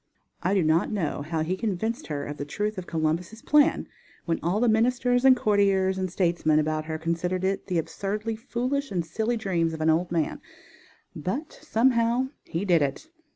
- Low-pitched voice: No, medium, 185 Hz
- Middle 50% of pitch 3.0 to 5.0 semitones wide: No, wide, 5.6 semitones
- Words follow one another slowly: No, average, 185 wpm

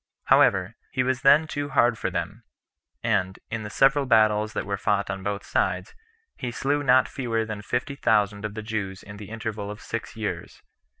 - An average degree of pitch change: Yes, average, 3.3 semitones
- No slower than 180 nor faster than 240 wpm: Yes, average, 190 wpm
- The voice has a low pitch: Yes, low, 110 Hz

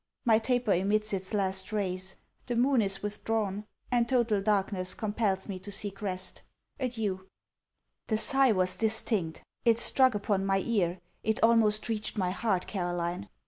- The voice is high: Yes, high, 205 Hz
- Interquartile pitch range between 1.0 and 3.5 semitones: Yes, average, 2.9 semitones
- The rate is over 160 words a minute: No, average, 150 wpm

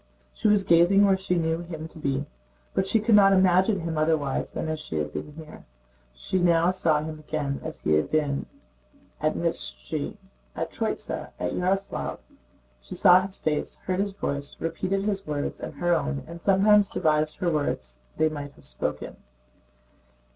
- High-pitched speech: No, medium, 165 Hz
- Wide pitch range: No, average, 4.3 semitones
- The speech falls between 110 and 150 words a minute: No, average, 175 wpm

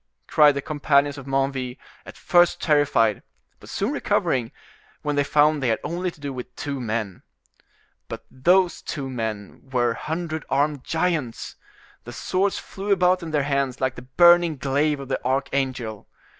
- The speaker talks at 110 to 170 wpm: Yes, average, 160 wpm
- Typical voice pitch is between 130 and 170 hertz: Yes, medium, 140 Hz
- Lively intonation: No, average, 3.4 semitones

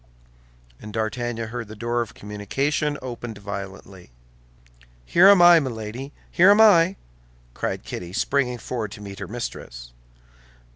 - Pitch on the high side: No, low, 120 Hz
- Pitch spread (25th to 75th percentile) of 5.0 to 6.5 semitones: Yes, wide, 5.4 semitones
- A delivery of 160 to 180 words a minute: No, slow, 135 wpm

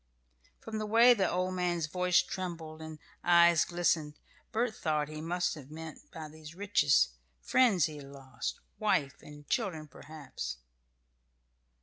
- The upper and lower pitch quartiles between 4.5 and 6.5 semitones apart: No, average, 3.3 semitones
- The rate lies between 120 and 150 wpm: Yes, average, 140 wpm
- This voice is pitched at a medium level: Yes, medium, 165 Hz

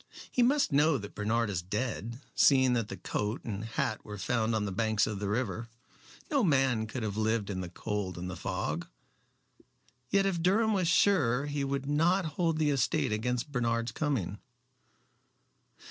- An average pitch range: No, wide, 5.8 semitones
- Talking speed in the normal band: Yes, average, 175 wpm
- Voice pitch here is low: Yes, low, 115 Hz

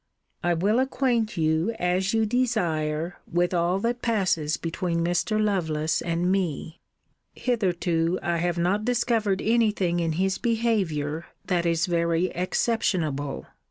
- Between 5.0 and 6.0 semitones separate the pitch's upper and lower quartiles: No, average, 4.4 semitones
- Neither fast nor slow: No, slow, 130 wpm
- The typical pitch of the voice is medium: Yes, medium, 180 Hz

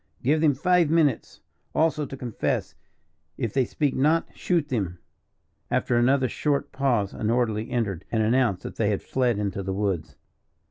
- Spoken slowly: No, average, 165 wpm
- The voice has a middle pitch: No, low, 125 Hz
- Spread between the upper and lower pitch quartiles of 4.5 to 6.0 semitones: Yes, wide, 5.4 semitones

